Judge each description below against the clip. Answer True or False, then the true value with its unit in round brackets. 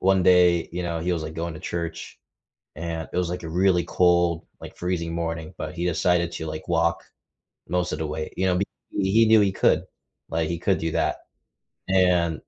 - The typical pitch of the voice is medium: False (85 Hz)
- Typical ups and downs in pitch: False (1.5 semitones)